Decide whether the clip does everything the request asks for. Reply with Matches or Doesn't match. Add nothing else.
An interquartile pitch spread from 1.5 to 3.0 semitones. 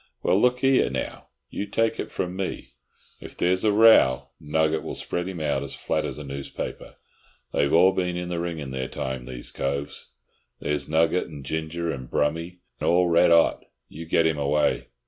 Doesn't match